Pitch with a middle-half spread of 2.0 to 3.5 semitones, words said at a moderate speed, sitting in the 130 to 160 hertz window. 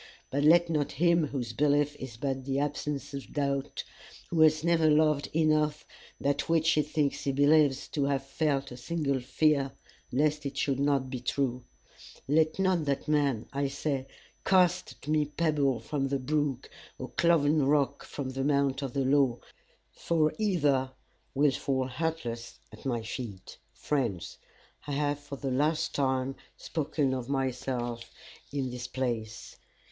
Yes: narrow, 2.5 semitones; average, 155 wpm; medium, 140 Hz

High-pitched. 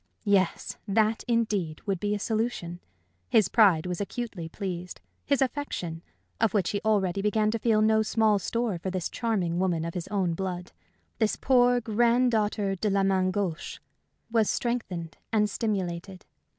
Yes: high, 205 Hz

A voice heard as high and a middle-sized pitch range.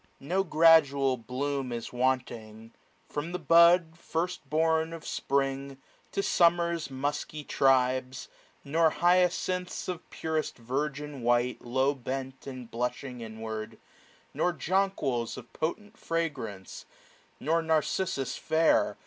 No: medium, 140 Hz; average, 4.6 semitones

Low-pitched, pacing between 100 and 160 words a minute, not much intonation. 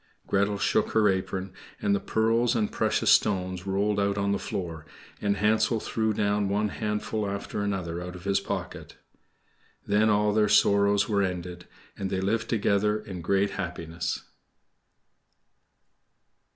Yes: low, 100 Hz; average, 145 wpm; narrow, 1.9 semitones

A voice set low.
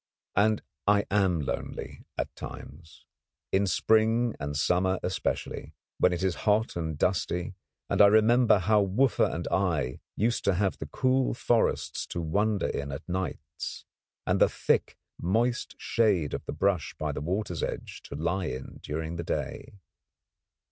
Yes: very low, 95 Hz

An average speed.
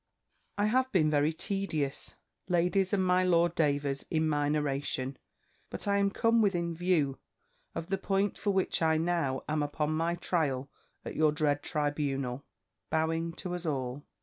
Yes: average, 160 wpm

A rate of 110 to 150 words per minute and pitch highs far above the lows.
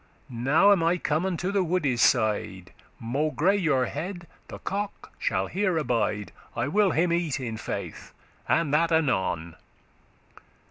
Yes: average, 140 wpm; wide, 7.0 semitones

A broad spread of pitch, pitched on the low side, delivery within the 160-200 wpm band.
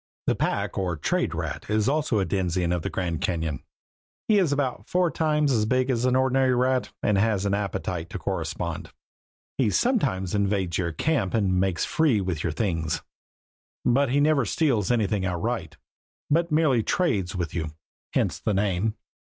Yes: wide, 6.3 semitones; low, 105 Hz; average, 170 wpm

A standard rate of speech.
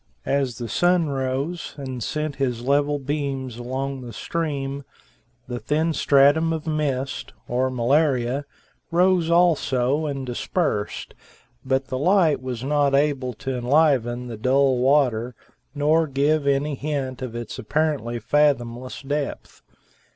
No: slow, 130 wpm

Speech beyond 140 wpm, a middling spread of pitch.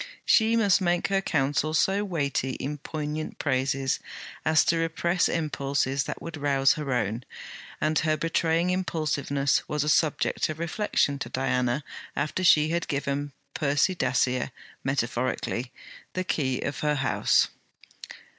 No: slow, 135 wpm; average, 3.3 semitones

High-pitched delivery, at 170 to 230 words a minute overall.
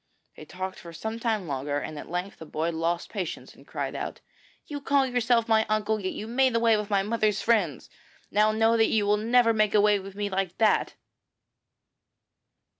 Yes: high, 210 Hz; average, 190 wpm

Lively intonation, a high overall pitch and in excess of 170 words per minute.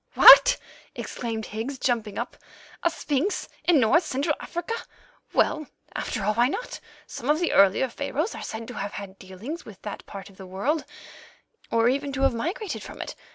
Yes: wide, 6.4 semitones; very high, 250 Hz; average, 180 wpm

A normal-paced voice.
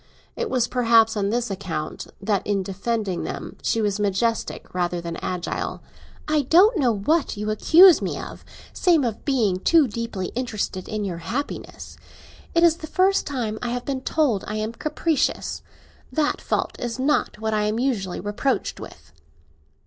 Yes: average, 165 wpm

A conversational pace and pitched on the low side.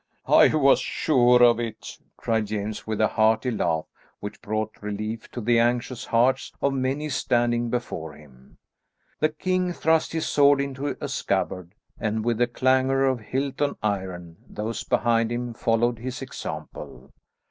Yes: average, 155 wpm; low, 120 Hz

